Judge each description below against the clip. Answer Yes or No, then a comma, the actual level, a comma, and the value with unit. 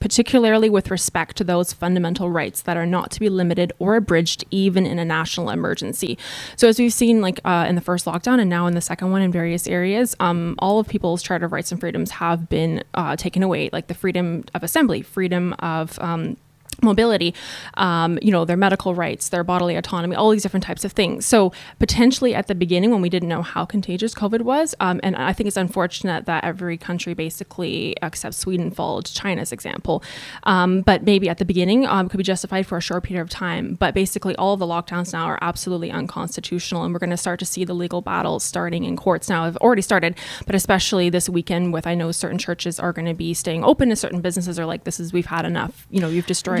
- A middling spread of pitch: No, narrow, 2.3 semitones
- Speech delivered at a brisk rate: Yes, fast, 230 wpm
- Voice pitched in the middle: Yes, medium, 180 Hz